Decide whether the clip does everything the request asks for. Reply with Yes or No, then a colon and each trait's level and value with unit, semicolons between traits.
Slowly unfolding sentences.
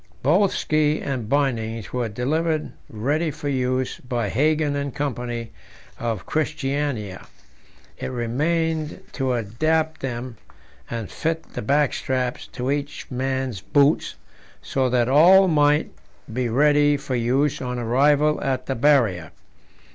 Yes: slow, 125 wpm